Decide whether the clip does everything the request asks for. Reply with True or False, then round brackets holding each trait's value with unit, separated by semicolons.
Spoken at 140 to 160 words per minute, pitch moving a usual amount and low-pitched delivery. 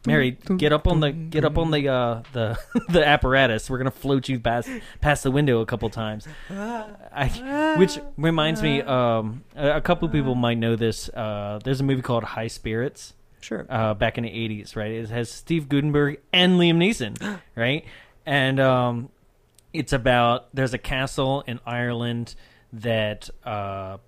False (170 wpm; 4.3 semitones; 130 Hz)